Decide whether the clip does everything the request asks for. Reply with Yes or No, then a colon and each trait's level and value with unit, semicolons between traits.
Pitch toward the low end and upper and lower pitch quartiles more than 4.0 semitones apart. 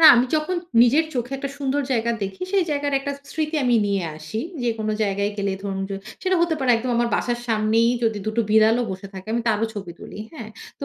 No: high, 230 Hz; average, 5.0 semitones